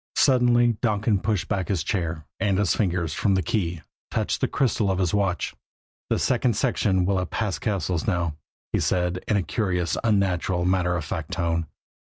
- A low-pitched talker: Yes, very low, 95 Hz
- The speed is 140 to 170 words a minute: No, average, 180 wpm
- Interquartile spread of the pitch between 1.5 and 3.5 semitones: Yes, average, 3.2 semitones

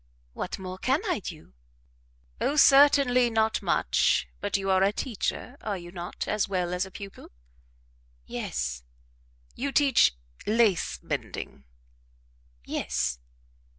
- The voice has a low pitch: No, high, 200 Hz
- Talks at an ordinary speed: No, slow, 120 wpm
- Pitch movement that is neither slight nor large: No, wide, 5.8 semitones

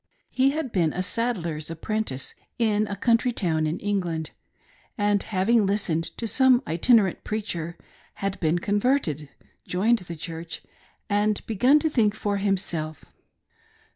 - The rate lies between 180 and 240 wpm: No, average, 140 wpm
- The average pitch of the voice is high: Yes, high, 200 Hz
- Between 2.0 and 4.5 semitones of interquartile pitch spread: No, average, 5.1 semitones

